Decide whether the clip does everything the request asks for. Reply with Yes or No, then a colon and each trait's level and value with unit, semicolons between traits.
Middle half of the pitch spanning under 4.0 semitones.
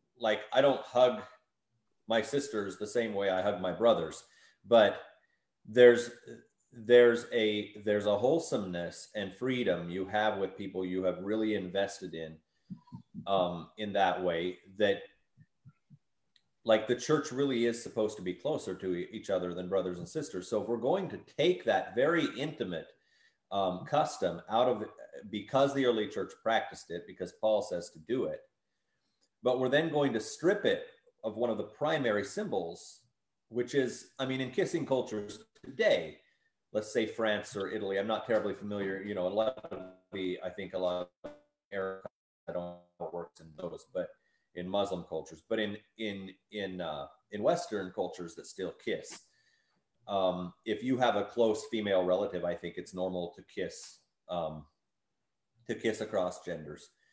No: average, 4.5 semitones